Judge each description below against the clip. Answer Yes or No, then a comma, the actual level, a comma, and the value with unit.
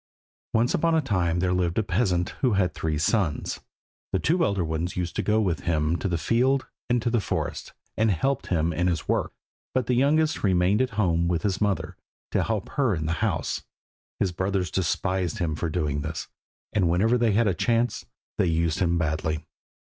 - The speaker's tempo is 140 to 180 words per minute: No, average, 200 wpm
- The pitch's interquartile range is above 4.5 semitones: Yes, average, 5.0 semitones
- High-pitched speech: No, very low, 95 Hz